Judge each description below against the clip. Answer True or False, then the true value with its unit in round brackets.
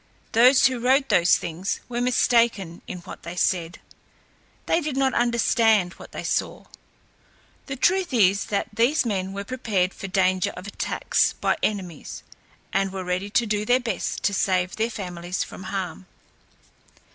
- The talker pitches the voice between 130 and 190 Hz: False (200 Hz)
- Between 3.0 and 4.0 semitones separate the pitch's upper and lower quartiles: False (4.6 semitones)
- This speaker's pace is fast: False (160 wpm)